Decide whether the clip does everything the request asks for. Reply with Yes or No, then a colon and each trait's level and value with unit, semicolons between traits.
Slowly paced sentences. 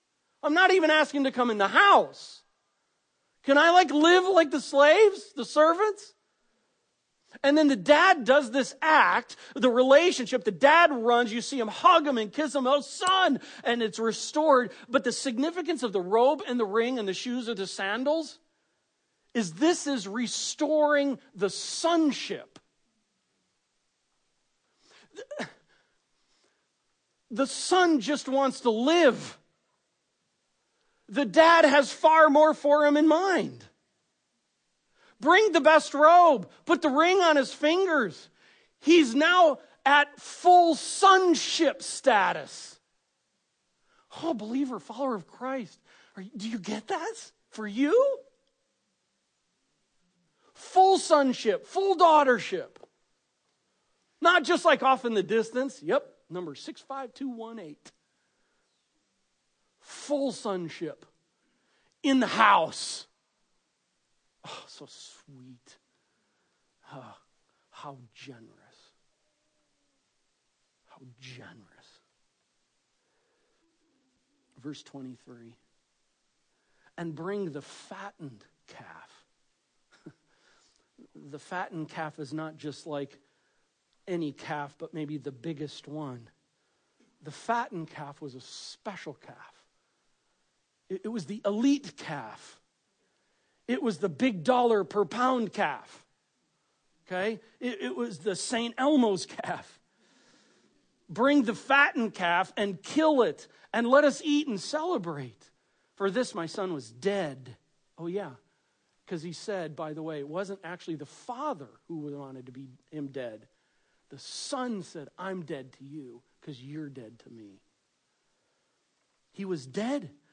Yes: slow, 115 wpm